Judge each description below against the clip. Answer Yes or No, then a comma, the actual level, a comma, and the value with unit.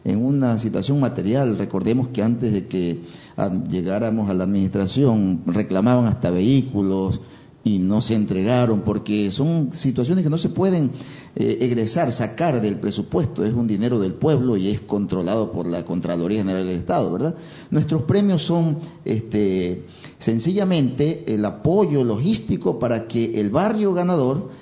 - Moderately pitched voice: No, low, 115 Hz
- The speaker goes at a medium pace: Yes, average, 145 wpm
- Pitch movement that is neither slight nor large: No, wide, 5.9 semitones